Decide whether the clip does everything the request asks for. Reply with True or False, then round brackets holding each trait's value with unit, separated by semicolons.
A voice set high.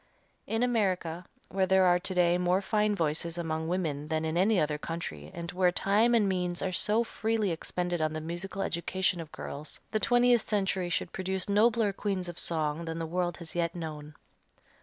False (180 Hz)